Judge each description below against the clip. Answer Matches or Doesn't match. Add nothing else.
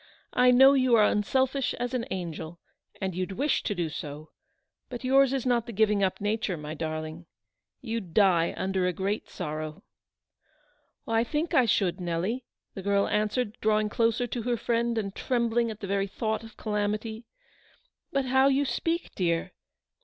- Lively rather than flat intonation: Doesn't match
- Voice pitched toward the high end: Matches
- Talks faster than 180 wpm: Doesn't match